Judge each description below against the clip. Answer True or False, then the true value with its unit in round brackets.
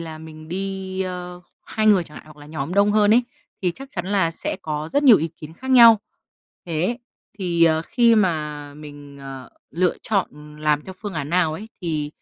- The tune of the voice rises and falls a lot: False (4.6 semitones)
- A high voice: False (170 Hz)